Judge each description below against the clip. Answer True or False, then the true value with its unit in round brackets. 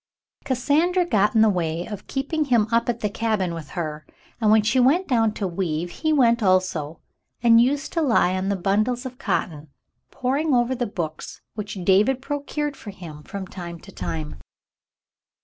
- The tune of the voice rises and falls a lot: True (6.3 semitones)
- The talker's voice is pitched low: False (215 Hz)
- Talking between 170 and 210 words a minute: True (180 wpm)